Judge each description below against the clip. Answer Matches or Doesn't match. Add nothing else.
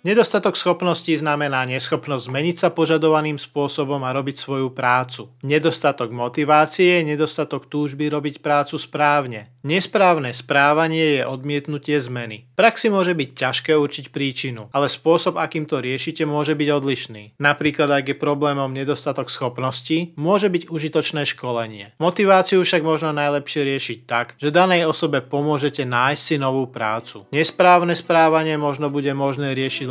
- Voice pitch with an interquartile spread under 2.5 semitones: Doesn't match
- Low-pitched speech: Doesn't match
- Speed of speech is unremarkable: Matches